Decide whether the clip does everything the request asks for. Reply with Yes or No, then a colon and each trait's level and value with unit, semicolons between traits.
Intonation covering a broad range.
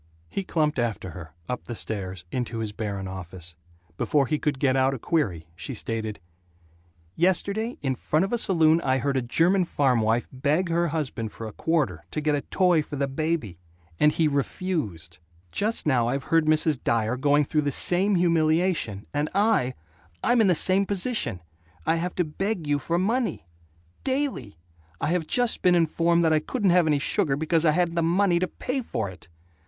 Yes: wide, 6.5 semitones